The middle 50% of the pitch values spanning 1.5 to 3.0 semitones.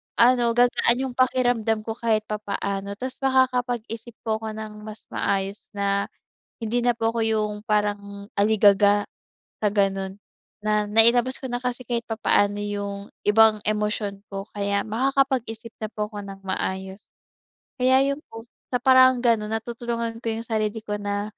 Yes: average, 2.7 semitones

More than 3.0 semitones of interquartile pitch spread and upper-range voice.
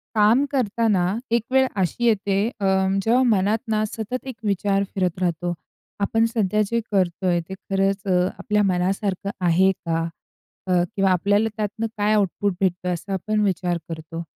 No: average, 2.7 semitones; high, 195 Hz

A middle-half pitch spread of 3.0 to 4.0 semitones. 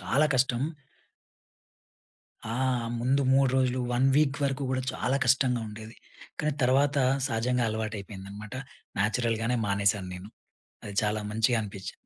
Yes: average, 3.7 semitones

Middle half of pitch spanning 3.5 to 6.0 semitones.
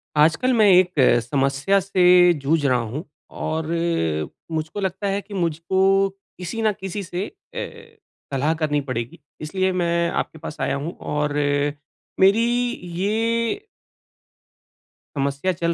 Yes: average, 4.7 semitones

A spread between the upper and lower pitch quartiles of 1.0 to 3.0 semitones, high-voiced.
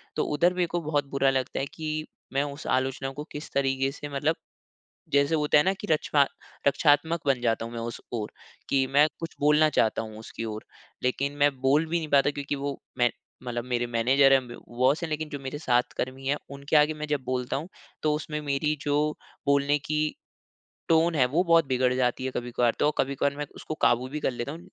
No: average, 2.7 semitones; medium, 140 Hz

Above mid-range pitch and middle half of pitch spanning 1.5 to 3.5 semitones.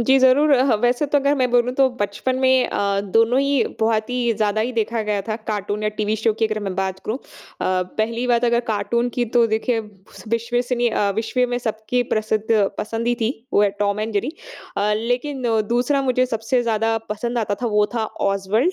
Yes: high, 230 Hz; average, 2.7 semitones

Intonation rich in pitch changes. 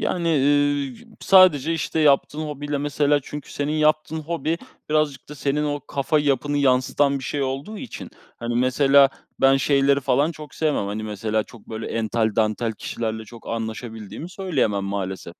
No: average, 4.3 semitones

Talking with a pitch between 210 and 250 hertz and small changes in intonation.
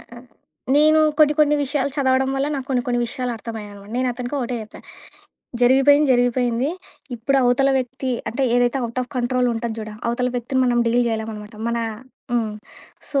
Yes: high, 245 Hz; narrow, 2.2 semitones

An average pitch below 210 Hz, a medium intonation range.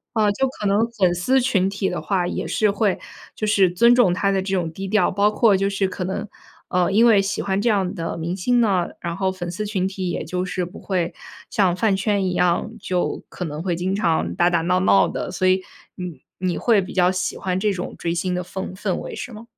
No: high, 190 Hz; narrow, 2.3 semitones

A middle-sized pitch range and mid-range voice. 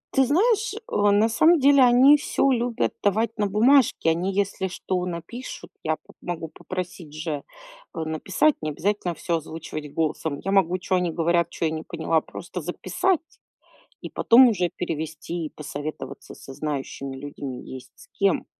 No: wide, 6.7 semitones; medium, 180 Hz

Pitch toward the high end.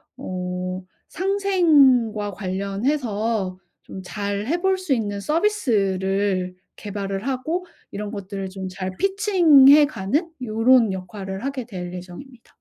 Yes: high, 210 Hz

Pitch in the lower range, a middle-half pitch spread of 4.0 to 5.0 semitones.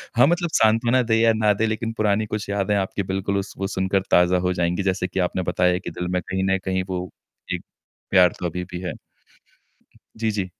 No: low, 100 Hz; average, 2.9 semitones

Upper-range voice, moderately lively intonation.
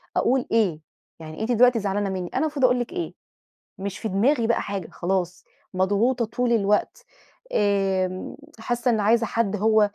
Yes: high, 215 Hz; average, 3.8 semitones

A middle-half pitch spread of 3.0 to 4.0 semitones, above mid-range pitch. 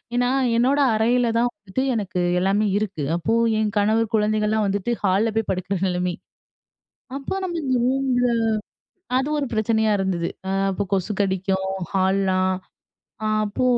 Yes: average, 3.5 semitones; high, 210 Hz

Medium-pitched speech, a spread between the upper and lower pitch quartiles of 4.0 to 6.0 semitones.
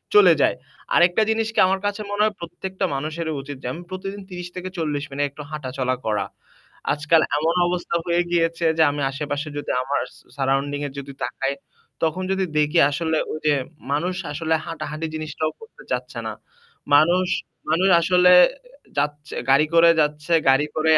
No: medium, 155 Hz; average, 3.5 semitones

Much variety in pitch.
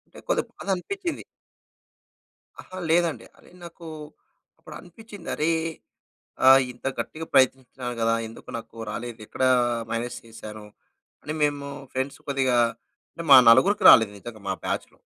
Yes: wide, 6.3 semitones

